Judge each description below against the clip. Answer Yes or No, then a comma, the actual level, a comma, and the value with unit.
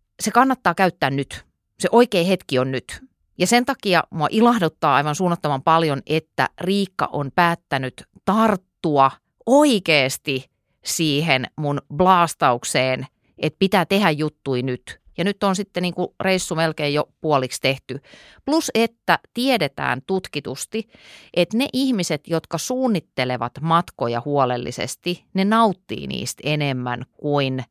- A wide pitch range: Yes, wide, 6.2 semitones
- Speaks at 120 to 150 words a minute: Yes, average, 125 wpm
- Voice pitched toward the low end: No, medium, 160 Hz